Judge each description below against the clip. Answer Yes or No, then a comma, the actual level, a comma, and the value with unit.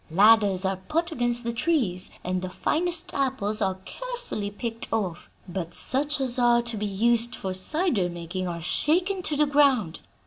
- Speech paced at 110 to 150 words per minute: No, average, 170 wpm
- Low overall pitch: No, high, 230 Hz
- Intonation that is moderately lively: No, wide, 7.6 semitones